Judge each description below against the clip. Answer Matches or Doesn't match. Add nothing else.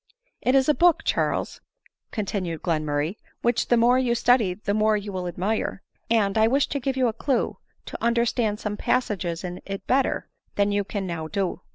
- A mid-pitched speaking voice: Doesn't match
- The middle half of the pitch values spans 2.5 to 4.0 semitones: Doesn't match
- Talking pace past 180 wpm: Matches